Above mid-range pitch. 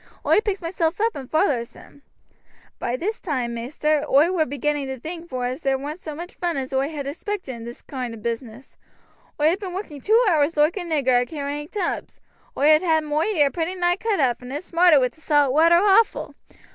Yes: very high, 300 Hz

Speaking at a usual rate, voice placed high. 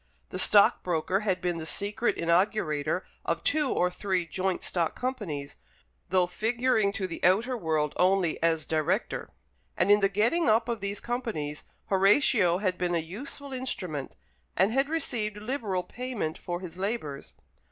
Yes: average, 150 wpm; high, 195 Hz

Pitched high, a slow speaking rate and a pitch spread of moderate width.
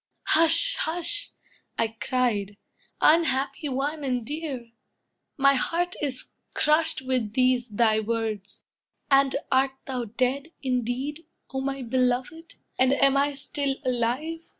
Yes: very high, 265 Hz; slow, 120 wpm; average, 3.1 semitones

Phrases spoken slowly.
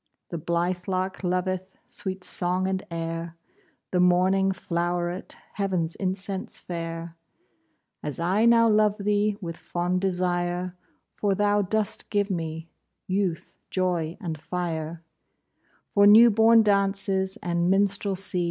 Yes: slow, 120 wpm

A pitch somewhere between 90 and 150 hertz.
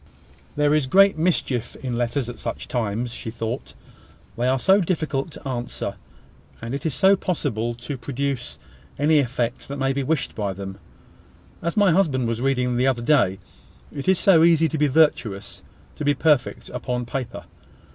Yes: low, 135 Hz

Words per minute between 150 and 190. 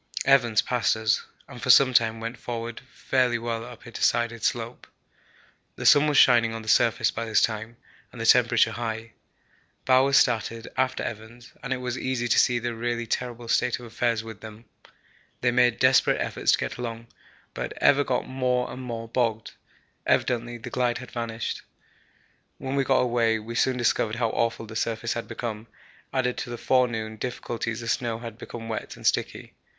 Yes: average, 185 wpm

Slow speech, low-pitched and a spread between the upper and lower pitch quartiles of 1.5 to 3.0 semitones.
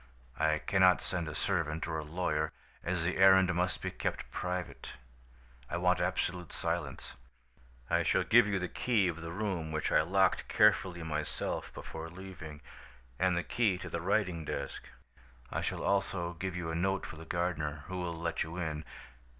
No: average, 175 wpm; very low, 85 Hz; narrow, 2.5 semitones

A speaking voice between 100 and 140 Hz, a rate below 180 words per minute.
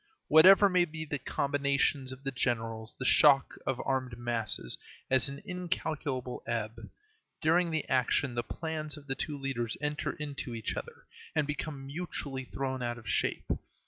Yes: low, 135 Hz; average, 160 wpm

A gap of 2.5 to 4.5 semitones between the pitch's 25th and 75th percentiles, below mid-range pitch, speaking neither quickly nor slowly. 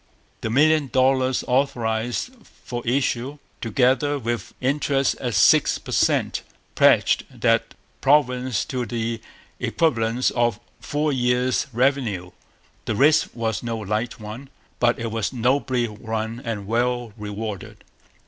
No: average, 2.9 semitones; low, 120 Hz; slow, 120 wpm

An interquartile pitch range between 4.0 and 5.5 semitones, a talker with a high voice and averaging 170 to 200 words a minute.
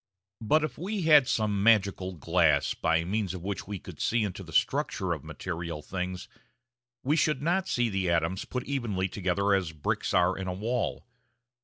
No: average, 4.9 semitones; very low, 95 Hz; average, 185 wpm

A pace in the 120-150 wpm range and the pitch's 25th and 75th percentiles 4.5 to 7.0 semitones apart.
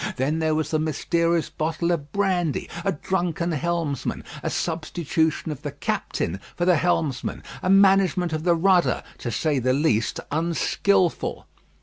No: average, 145 wpm; average, 2.7 semitones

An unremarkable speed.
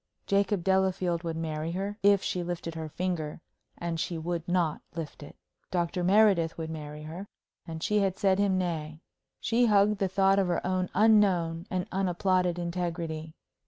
Yes: average, 165 wpm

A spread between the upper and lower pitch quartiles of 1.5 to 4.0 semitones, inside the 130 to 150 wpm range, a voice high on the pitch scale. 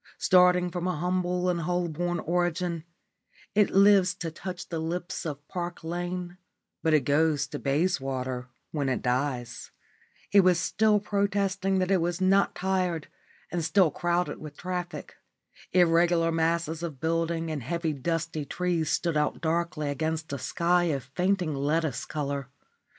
No: average, 2.7 semitones; average, 145 wpm; medium, 170 Hz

